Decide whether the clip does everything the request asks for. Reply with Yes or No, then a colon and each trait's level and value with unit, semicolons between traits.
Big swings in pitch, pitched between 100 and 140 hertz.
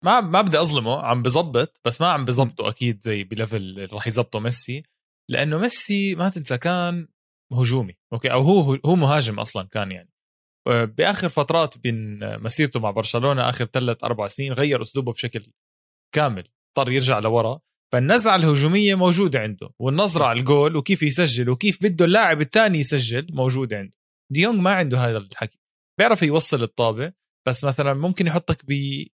Yes: wide, 5.9 semitones; low, 135 Hz